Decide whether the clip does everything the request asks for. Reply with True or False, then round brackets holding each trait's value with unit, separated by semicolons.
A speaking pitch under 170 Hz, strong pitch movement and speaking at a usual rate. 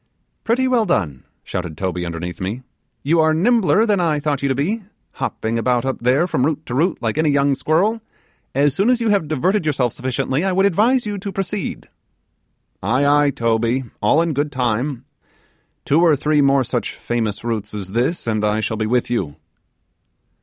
True (140 Hz; 6.8 semitones; 190 wpm)